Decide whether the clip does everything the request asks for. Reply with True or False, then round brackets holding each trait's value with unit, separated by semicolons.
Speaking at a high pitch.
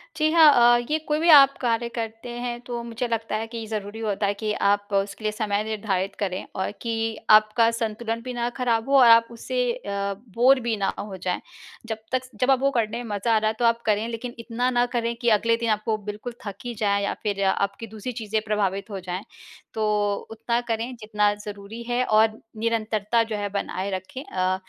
True (225 Hz)